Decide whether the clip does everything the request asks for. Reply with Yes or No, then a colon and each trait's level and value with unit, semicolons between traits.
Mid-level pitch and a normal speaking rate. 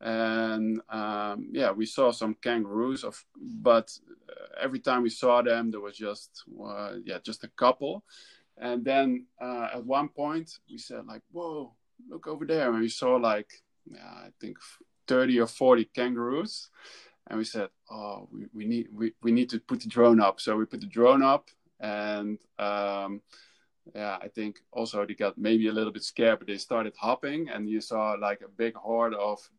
No: low, 115 Hz; average, 185 wpm